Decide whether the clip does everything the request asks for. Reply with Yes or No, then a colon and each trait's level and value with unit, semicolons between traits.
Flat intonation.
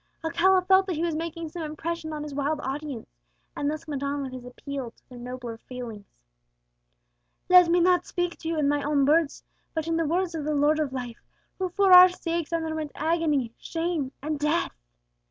No: average, 3.2 semitones